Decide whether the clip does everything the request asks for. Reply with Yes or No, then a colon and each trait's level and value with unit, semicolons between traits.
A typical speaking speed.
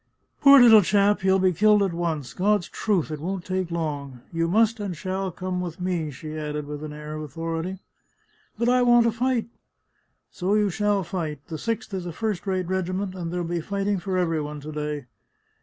No: fast, 215 wpm